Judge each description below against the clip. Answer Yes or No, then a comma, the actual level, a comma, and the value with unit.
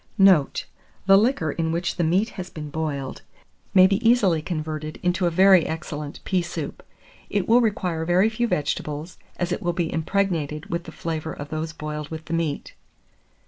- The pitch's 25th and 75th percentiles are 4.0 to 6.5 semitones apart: No, average, 3.3 semitones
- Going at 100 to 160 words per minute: No, average, 180 wpm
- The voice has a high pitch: No, medium, 165 Hz